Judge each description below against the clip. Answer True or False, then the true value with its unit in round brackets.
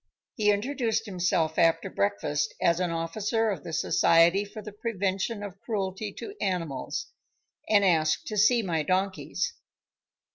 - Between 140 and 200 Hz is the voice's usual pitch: True (190 Hz)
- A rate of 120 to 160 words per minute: True (140 wpm)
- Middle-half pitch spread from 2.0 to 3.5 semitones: False (4.2 semitones)